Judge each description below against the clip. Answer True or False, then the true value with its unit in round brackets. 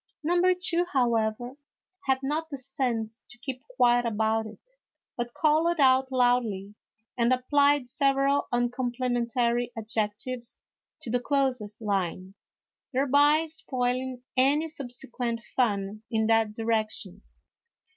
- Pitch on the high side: True (245 Hz)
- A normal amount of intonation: True (3.5 semitones)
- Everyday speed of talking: False (110 wpm)